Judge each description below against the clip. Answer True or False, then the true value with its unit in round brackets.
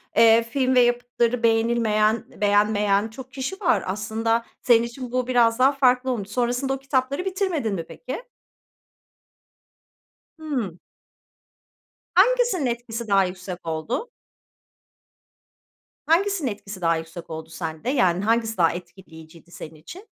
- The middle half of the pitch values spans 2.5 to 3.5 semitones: False (4.8 semitones)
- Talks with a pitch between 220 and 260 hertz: True (230 Hz)